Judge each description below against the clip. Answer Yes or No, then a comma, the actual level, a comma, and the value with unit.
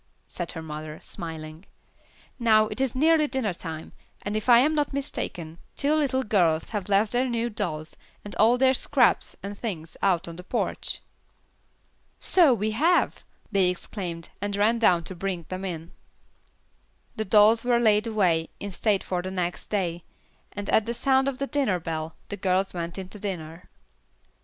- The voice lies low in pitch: No, high, 205 Hz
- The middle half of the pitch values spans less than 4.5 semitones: No, wide, 5.4 semitones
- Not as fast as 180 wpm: Yes, average, 170 wpm